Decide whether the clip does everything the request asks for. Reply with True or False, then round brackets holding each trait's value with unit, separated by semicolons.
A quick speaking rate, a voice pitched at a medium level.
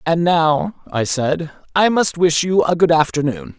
False (185 wpm; 155 Hz)